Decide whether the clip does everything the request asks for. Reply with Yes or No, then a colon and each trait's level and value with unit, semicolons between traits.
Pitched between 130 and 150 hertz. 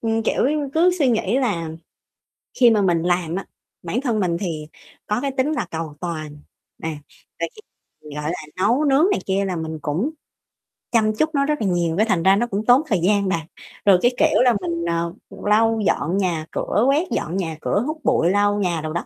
No: high, 200 Hz